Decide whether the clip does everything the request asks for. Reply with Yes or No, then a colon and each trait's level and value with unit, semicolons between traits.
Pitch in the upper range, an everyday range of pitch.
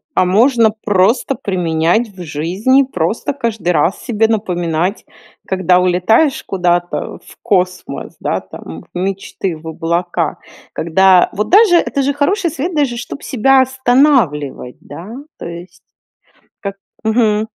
No: high, 195 Hz; wide, 6.1 semitones